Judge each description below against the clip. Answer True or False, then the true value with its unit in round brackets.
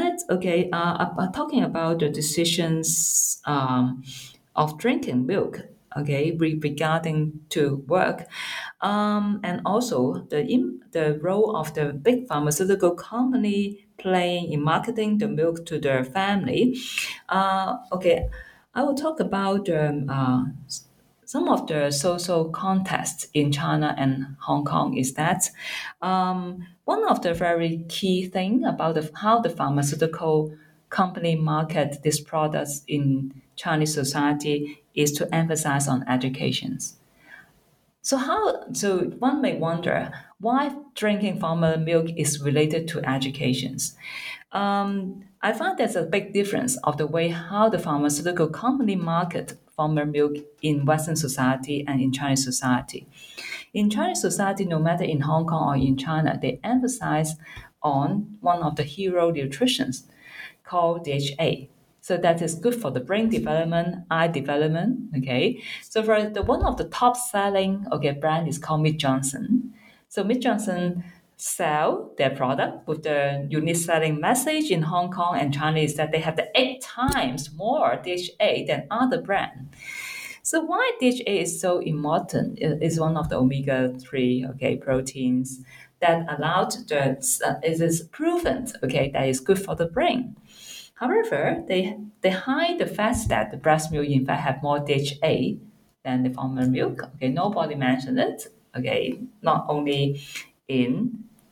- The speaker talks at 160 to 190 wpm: False (145 wpm)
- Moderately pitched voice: True (165 Hz)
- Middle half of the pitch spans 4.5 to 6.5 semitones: True (5.4 semitones)